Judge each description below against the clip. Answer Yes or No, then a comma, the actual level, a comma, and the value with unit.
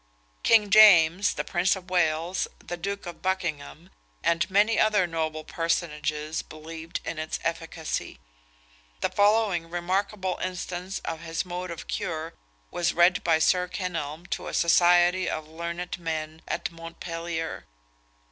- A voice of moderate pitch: Yes, medium, 170 Hz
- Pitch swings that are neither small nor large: No, narrow, 2.3 semitones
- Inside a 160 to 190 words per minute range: No, slow, 135 wpm